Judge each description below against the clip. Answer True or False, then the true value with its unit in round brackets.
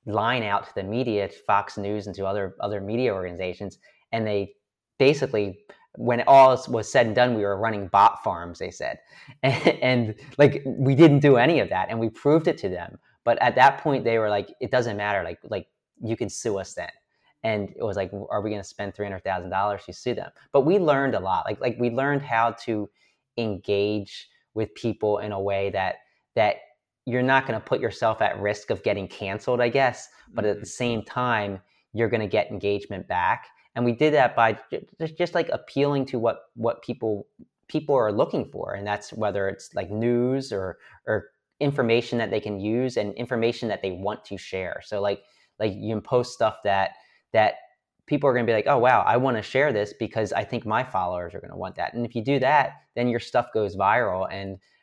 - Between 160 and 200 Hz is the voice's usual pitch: False (110 Hz)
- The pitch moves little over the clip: False (3.8 semitones)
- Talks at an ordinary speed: False (215 wpm)